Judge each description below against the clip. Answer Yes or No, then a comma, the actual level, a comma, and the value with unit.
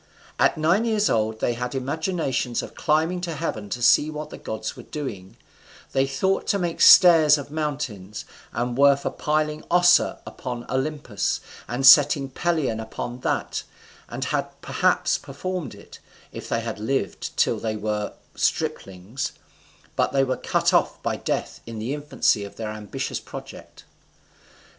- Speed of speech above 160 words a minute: No, average, 155 wpm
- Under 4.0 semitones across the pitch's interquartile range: No, wide, 5.5 semitones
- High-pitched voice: No, low, 135 Hz